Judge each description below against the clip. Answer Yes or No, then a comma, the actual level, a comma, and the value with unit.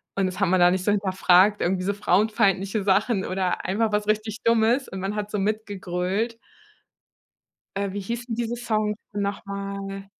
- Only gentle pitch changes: Yes, narrow, 2.2 semitones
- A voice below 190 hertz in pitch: No, high, 200 Hz